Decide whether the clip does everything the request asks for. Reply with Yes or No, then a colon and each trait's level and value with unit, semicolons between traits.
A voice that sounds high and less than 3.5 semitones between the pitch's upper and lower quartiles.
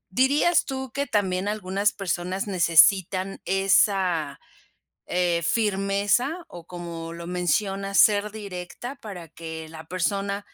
Yes: high, 195 Hz; average, 2.8 semitones